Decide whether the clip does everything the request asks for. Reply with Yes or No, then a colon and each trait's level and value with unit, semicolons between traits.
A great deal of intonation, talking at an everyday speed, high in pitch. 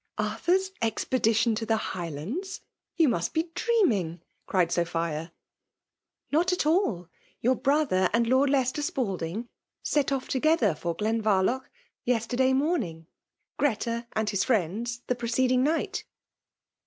Yes: wide, 6.5 semitones; average, 145 wpm; high, 235 Hz